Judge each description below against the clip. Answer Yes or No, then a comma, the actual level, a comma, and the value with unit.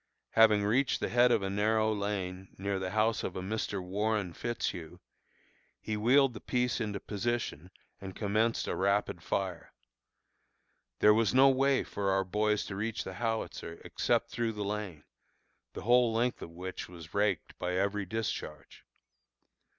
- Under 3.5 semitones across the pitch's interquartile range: Yes, average, 2.9 semitones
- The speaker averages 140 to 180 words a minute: Yes, average, 160 wpm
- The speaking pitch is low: Yes, low, 105 Hz